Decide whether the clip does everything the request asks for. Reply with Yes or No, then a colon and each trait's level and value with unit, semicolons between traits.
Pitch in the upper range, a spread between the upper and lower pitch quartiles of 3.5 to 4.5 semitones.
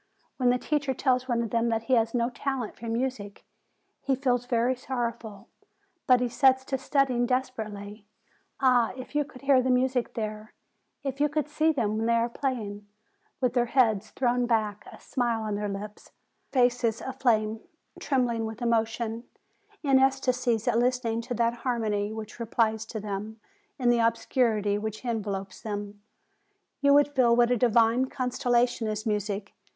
No: high, 235 Hz; average, 2.7 semitones